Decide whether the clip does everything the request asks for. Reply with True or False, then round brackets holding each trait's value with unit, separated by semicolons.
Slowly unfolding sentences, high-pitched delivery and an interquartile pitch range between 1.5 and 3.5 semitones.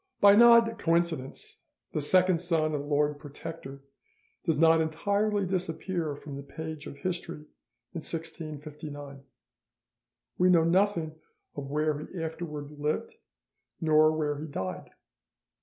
False (125 wpm; 160 Hz; 3.0 semitones)